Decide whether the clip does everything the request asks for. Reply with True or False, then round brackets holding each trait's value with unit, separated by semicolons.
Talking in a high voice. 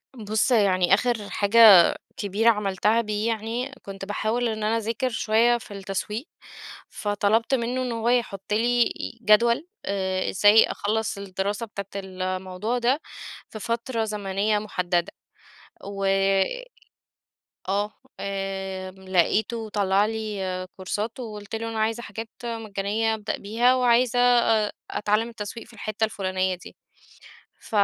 True (215 Hz)